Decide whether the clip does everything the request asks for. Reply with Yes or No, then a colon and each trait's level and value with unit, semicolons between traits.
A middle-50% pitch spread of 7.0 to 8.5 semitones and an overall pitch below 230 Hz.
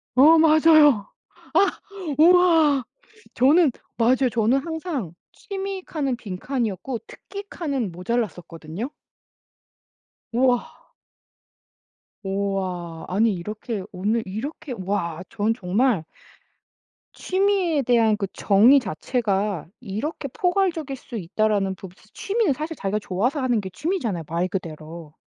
No: wide, 7.6 semitones; high, 235 Hz